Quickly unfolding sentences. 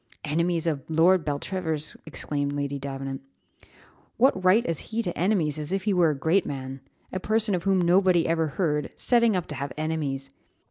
No: average, 180 wpm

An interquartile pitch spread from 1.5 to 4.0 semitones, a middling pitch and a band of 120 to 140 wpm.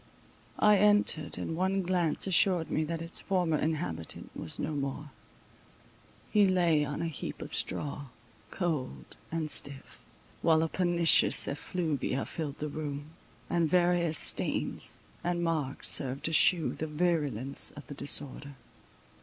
Yes: average, 3.3 semitones; medium, 160 Hz; slow, 135 wpm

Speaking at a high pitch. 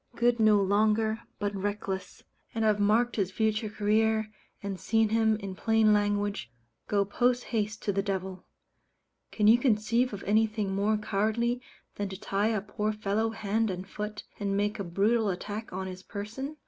Yes: high, 210 Hz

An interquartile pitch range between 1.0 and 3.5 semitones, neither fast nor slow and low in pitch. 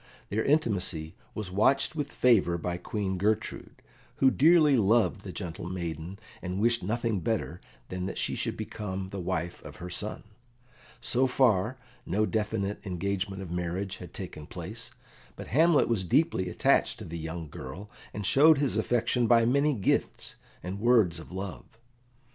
No: average, 4.8 semitones; average, 160 wpm; low, 100 Hz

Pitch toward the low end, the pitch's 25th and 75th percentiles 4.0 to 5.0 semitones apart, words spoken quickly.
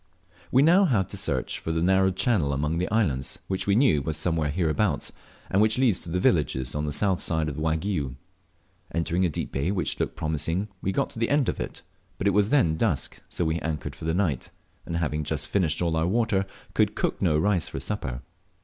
Yes: very low, 85 Hz; average, 4.6 semitones; fast, 215 wpm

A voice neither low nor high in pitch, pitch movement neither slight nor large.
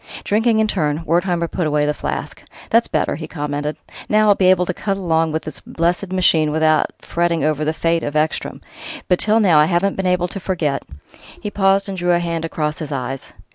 Yes: medium, 170 Hz; average, 3.6 semitones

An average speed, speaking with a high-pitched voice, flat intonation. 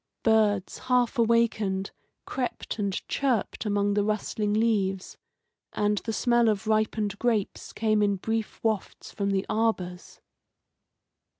No: slow, 120 wpm; high, 215 Hz; narrow, 1.9 semitones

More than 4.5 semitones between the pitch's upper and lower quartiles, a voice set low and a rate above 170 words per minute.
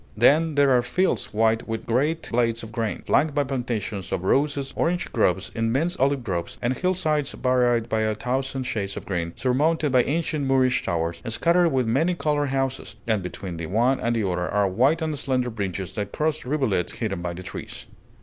Yes: average, 5.1 semitones; low, 125 Hz; average, 190 wpm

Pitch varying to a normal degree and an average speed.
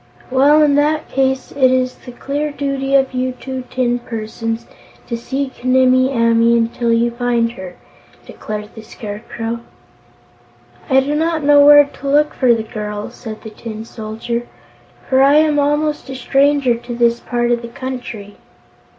Yes: average, 3.0 semitones; average, 160 wpm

